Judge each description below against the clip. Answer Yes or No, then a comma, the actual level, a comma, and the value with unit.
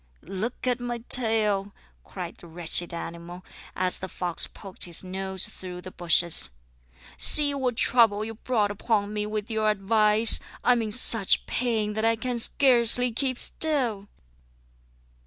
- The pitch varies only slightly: No, average, 3.9 semitones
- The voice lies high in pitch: Yes, high, 215 Hz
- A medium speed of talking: Yes, average, 150 wpm